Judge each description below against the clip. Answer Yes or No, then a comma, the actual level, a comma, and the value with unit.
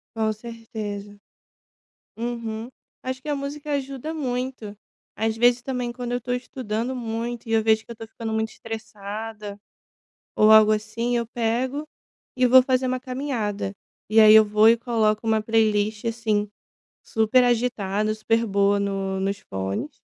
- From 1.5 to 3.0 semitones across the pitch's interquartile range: Yes, narrow, 2.5 semitones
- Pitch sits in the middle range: No, high, 225 Hz